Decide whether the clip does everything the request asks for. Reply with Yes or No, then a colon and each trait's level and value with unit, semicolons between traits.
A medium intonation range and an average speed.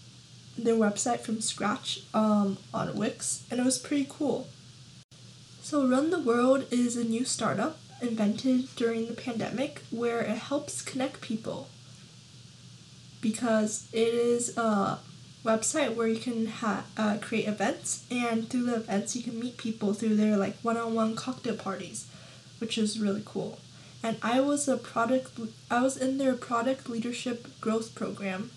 No: narrow, 2.2 semitones; average, 160 wpm